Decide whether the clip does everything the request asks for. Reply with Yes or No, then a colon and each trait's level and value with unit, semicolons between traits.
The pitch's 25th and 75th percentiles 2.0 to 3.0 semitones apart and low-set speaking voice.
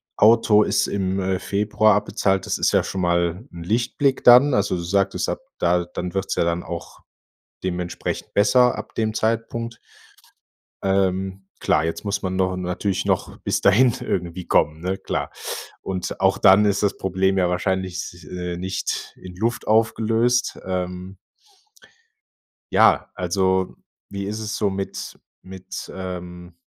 Yes: average, 2.7 semitones; very low, 95 Hz